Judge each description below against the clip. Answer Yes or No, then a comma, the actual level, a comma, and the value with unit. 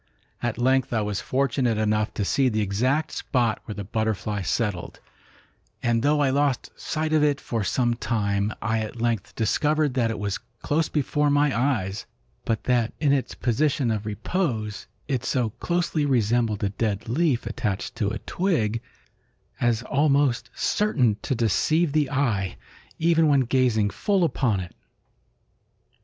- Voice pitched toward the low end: Yes, low, 120 Hz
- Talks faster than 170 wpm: No, average, 155 wpm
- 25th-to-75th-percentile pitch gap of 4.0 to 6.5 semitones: Yes, average, 4.8 semitones